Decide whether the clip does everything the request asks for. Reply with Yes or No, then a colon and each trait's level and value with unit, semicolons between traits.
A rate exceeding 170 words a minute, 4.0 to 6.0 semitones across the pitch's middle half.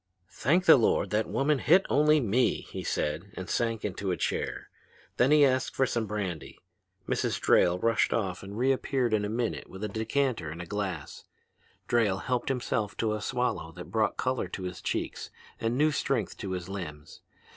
Yes: average, 180 wpm; average, 5.2 semitones